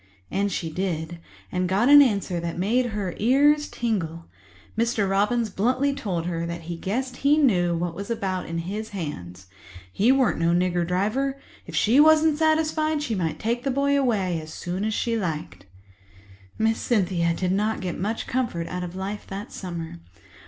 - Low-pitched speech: No, high, 200 Hz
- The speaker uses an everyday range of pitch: No, wide, 6.0 semitones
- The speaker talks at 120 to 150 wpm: No, average, 170 wpm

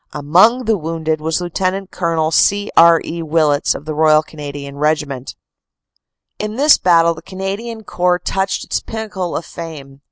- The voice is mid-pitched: Yes, medium, 165 Hz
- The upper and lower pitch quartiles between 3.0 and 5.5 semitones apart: Yes, average, 3.9 semitones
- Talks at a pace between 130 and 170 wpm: Yes, average, 160 wpm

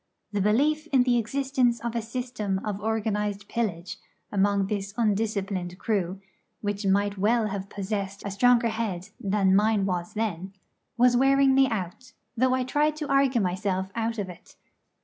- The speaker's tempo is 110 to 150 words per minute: No, average, 160 wpm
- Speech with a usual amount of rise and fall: Yes, average, 3.7 semitones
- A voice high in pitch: Yes, high, 210 Hz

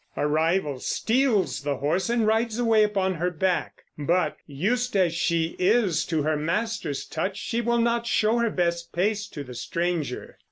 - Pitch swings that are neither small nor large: No, wide, 5.8 semitones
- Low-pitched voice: No, medium, 185 Hz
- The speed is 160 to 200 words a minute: Yes, average, 170 wpm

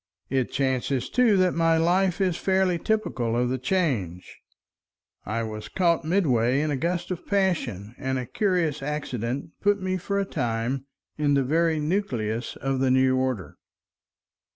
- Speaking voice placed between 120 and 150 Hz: Yes, medium, 140 Hz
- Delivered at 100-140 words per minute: No, average, 155 wpm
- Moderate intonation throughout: No, wide, 6.4 semitones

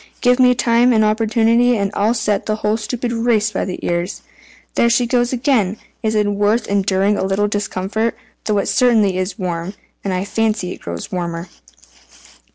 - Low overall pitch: No, high, 215 Hz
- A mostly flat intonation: No, average, 3.2 semitones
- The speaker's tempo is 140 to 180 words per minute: Yes, average, 175 wpm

